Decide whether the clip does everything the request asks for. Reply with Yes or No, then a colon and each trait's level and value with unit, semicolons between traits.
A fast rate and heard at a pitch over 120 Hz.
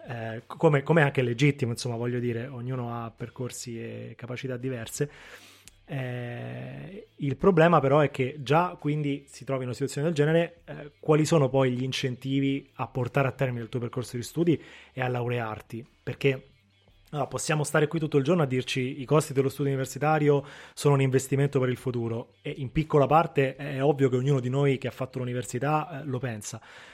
Yes: fast, 190 wpm; low, 135 Hz